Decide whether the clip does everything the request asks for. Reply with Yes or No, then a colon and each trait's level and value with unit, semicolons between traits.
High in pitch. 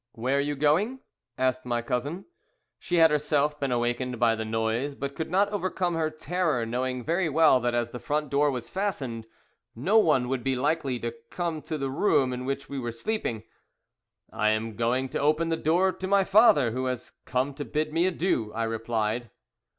No: medium, 140 Hz